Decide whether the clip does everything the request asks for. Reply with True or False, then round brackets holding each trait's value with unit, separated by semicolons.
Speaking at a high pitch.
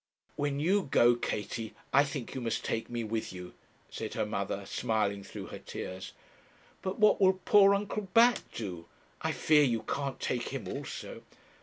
False (125 Hz)